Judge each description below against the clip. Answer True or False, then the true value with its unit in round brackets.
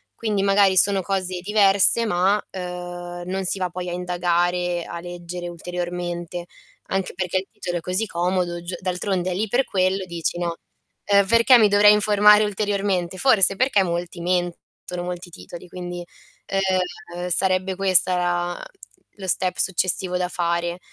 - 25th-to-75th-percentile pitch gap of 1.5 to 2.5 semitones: True (1.8 semitones)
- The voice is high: False (180 Hz)